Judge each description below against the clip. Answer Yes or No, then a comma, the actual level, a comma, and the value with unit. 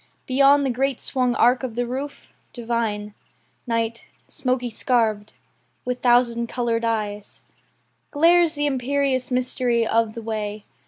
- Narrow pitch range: Yes, narrow, 2.3 semitones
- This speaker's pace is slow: Yes, slow, 125 wpm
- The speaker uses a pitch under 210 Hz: No, high, 245 Hz